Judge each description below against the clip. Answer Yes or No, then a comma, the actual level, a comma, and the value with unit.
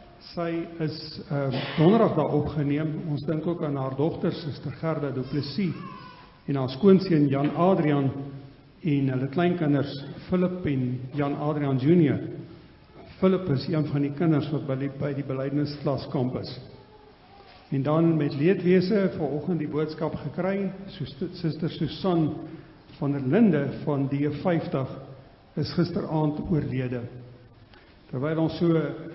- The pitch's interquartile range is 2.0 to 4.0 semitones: Yes, average, 3.1 semitones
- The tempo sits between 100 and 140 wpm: Yes, slow, 135 wpm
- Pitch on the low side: No, medium, 150 Hz